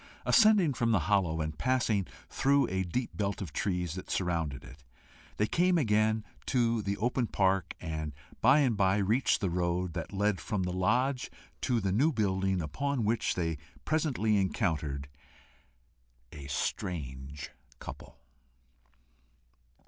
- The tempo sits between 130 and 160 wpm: Yes, average, 140 wpm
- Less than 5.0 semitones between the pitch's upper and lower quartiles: No, wide, 5.5 semitones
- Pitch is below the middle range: Yes, low, 100 Hz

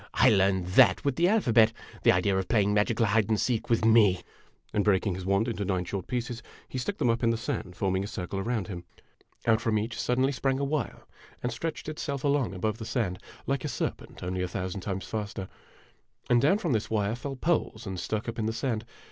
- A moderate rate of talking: No, fast, 230 wpm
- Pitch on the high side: No, low, 110 Hz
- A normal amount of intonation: Yes, average, 4.2 semitones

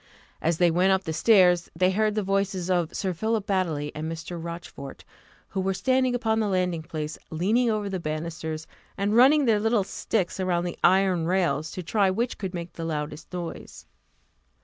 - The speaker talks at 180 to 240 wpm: Yes, average, 185 wpm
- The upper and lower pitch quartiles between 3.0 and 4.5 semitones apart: Yes, average, 3.7 semitones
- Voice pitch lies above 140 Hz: Yes, medium, 185 Hz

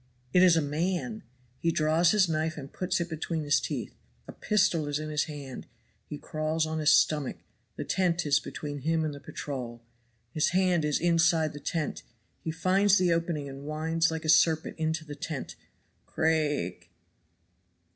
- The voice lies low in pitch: No, medium, 160 Hz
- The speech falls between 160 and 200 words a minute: Yes, average, 175 wpm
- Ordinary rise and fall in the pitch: No, narrow, 2.3 semitones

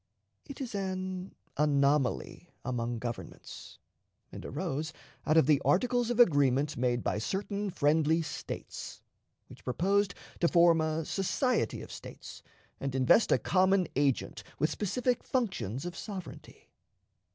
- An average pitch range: No, wide, 5.9 semitones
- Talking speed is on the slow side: Yes, slow, 130 wpm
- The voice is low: No, medium, 165 Hz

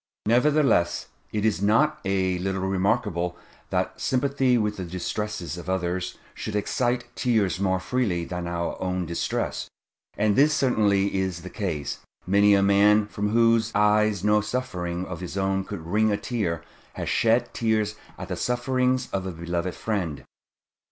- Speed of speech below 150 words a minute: No, average, 155 wpm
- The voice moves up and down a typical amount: Yes, average, 3.7 semitones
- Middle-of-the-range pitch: No, low, 100 Hz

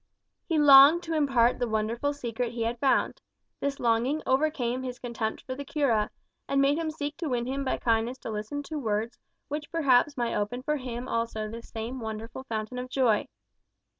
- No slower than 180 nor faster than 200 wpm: Yes, average, 190 wpm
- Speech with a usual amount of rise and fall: Yes, average, 3.6 semitones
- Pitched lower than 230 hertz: No, very high, 250 Hz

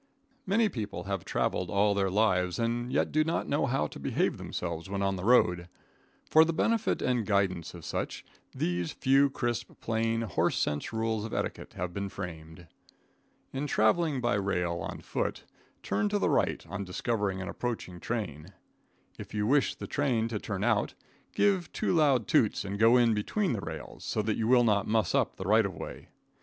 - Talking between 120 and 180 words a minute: No, average, 190 wpm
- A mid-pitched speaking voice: No, low, 110 Hz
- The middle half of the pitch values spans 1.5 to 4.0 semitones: No, average, 4.5 semitones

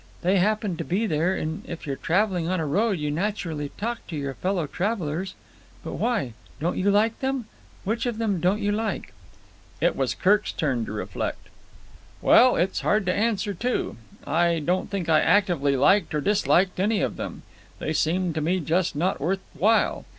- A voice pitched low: No, medium, 185 Hz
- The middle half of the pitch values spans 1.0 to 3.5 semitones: No, average, 4.5 semitones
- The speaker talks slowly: No, average, 185 wpm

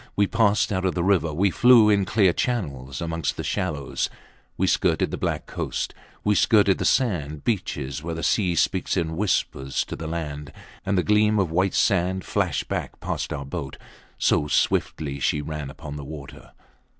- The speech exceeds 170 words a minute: Yes, average, 180 wpm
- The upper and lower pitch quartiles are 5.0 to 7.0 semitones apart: Yes, average, 5.3 semitones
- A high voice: No, very low, 85 Hz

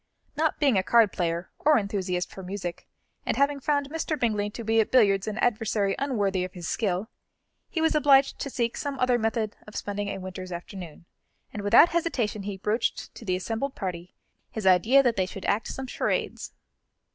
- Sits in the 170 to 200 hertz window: No, high, 215 Hz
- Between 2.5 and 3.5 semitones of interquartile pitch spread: No, wide, 5.4 semitones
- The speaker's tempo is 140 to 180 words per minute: No, average, 190 wpm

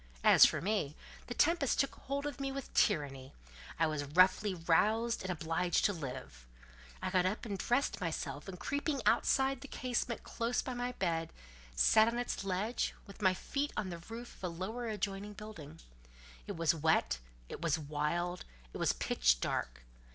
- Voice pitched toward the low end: No, high, 190 Hz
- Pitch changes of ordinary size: No, wide, 6.6 semitones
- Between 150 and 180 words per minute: Yes, average, 175 wpm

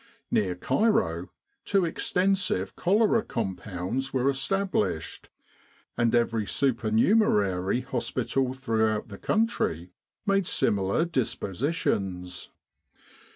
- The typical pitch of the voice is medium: No, low, 120 Hz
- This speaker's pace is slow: Yes, slow, 80 wpm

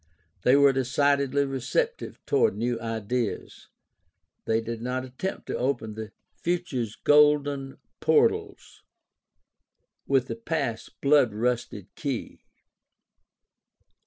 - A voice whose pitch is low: Yes, low, 130 Hz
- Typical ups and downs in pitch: Yes, average, 3.6 semitones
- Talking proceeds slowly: Yes, slow, 100 wpm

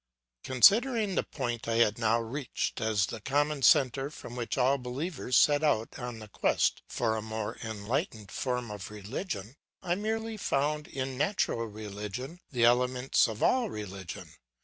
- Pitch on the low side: Yes, low, 125 Hz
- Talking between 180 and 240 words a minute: No, average, 155 wpm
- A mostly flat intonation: No, average, 4.9 semitones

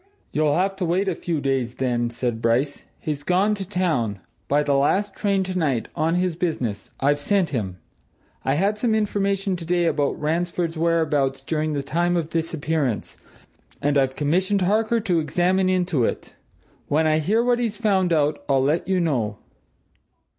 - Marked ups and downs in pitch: No, average, 4.8 semitones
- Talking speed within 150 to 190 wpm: Yes, average, 170 wpm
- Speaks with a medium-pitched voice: Yes, medium, 165 Hz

